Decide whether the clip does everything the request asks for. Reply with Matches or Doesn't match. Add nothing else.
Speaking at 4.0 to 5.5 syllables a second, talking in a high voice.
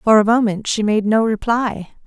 Matches